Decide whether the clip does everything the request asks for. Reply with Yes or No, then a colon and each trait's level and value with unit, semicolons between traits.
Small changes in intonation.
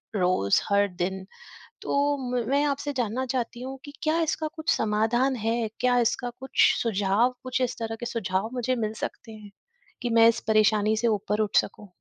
No: average, 3.4 semitones